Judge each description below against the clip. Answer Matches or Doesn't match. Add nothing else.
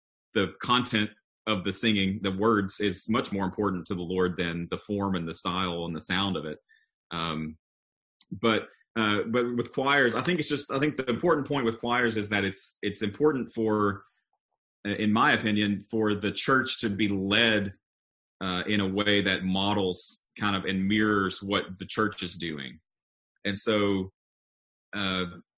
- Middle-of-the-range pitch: Doesn't match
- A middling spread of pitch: Matches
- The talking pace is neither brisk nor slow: Matches